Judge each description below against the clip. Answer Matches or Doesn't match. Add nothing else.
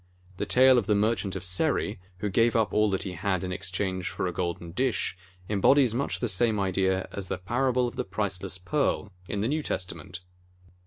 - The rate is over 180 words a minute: Matches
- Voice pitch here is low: Matches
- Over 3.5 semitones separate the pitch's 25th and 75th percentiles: Matches